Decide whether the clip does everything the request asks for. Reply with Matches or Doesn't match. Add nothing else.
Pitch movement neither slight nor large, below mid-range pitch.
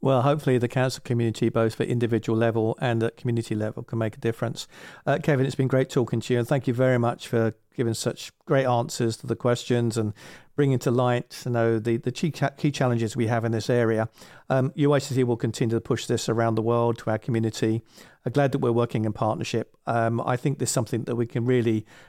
Doesn't match